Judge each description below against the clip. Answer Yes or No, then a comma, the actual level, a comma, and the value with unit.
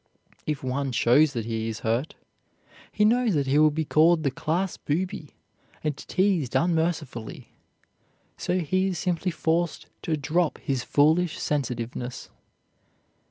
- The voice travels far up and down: No, average, 4.7 semitones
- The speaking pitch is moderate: Yes, medium, 155 Hz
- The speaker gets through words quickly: No, slow, 135 wpm